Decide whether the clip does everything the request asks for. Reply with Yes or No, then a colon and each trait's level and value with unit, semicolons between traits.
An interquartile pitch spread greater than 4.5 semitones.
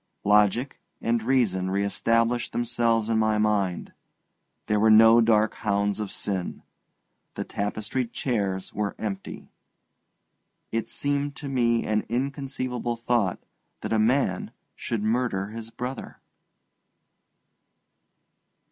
No: average, 2.7 semitones